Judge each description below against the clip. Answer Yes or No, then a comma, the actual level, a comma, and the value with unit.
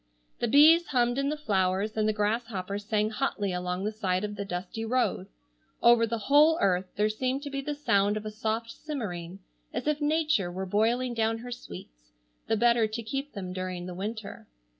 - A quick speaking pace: No, average, 195 wpm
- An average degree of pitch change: Yes, average, 4.1 semitones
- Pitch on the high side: Yes, high, 220 Hz